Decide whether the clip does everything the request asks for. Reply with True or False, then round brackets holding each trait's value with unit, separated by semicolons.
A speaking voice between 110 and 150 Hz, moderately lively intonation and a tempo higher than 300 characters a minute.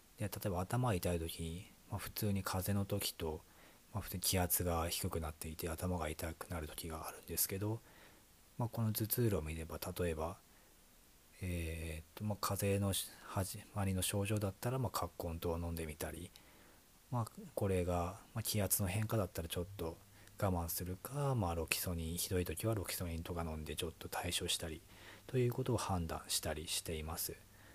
False (90 Hz; 3.8 semitones; 350 characters per minute)